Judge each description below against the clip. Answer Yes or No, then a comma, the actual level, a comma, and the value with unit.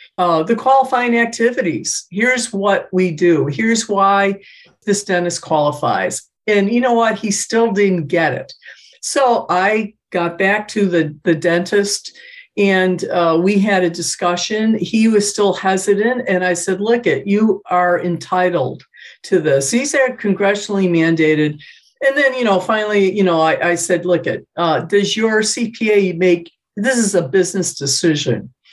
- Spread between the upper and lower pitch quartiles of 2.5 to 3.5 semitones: No, average, 3.9 semitones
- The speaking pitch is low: No, high, 195 Hz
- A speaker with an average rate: Yes, average, 160 wpm